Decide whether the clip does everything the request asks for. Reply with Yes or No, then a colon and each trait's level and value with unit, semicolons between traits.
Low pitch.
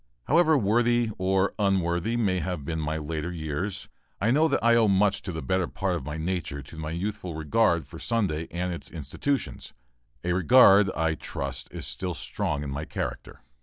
Yes: very low, 90 Hz